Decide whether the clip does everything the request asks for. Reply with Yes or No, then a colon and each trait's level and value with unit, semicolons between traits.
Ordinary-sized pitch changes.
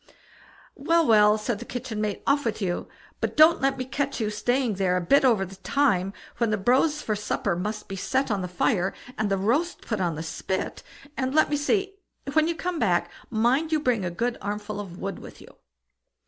No: wide, 6.0 semitones